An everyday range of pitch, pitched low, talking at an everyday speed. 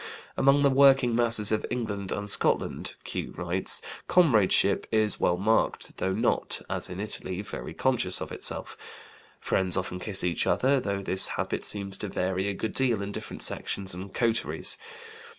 Yes: average, 3.6 semitones; low, 105 Hz; average, 165 wpm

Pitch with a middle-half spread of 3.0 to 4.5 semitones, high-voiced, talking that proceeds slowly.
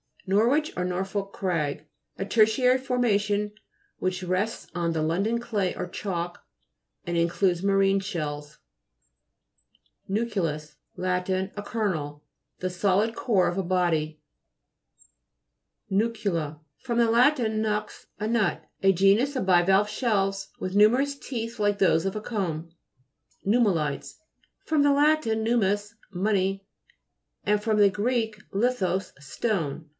Yes: average, 3.6 semitones; high, 195 Hz; slow, 125 wpm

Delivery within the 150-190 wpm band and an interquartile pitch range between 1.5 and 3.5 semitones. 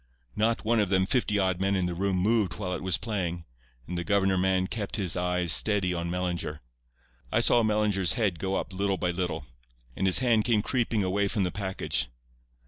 No: fast, 205 wpm; average, 2.7 semitones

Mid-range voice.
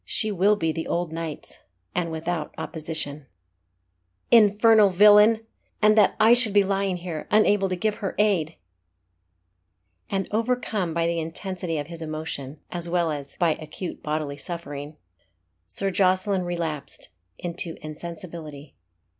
Yes: medium, 175 Hz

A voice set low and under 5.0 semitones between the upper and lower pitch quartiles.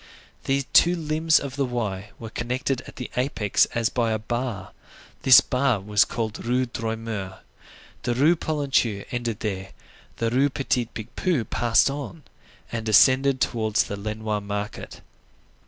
Yes: low, 120 Hz; average, 3.7 semitones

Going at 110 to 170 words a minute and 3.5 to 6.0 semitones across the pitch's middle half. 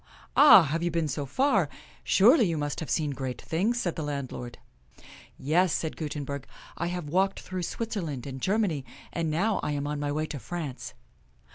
No: average, 190 wpm; average, 4.3 semitones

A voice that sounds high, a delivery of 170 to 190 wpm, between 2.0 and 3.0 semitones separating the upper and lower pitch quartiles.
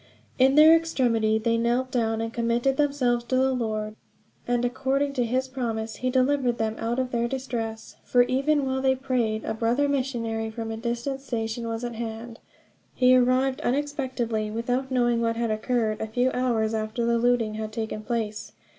Yes: high, 240 Hz; average, 180 wpm; narrow, 2.6 semitones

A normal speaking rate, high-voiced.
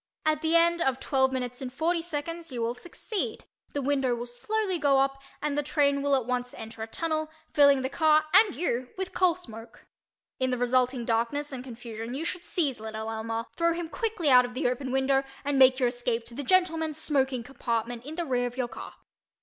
No: fast, 215 wpm; very high, 270 Hz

